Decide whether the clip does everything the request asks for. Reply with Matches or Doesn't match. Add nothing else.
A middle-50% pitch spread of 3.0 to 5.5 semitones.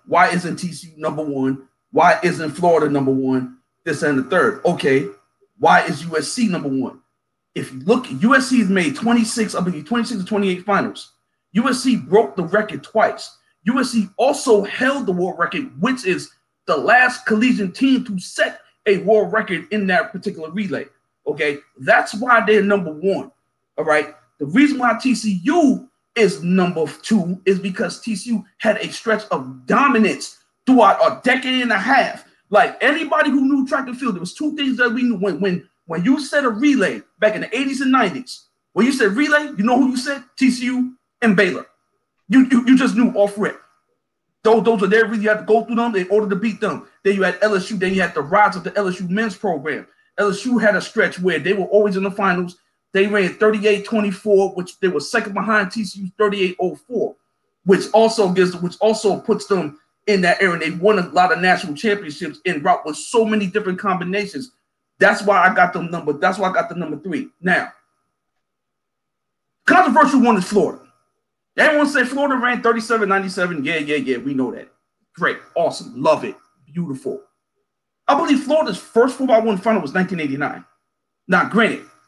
Matches